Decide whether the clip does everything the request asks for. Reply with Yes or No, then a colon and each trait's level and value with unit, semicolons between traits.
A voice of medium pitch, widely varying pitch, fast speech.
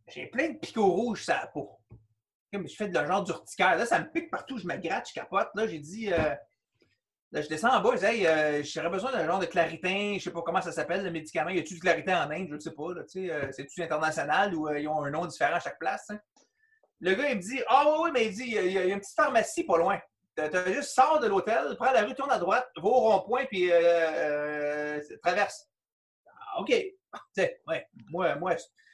Yes: medium, 180 Hz; wide, 6.5 semitones; fast, 255 wpm